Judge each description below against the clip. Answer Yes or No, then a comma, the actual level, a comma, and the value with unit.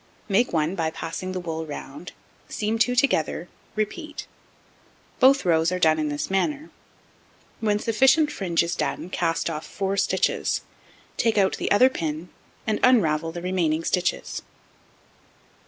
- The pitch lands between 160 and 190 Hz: Yes, medium, 185 Hz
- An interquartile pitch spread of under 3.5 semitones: No, average, 5.1 semitones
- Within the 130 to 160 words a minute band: Yes, average, 140 wpm